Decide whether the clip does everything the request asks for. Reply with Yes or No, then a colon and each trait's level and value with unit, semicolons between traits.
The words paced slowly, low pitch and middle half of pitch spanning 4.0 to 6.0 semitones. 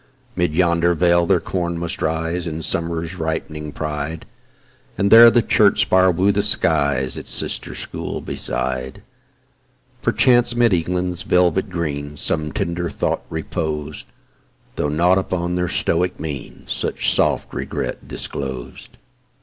No: slow, 130 wpm; very low, 85 Hz; average, 2.7 semitones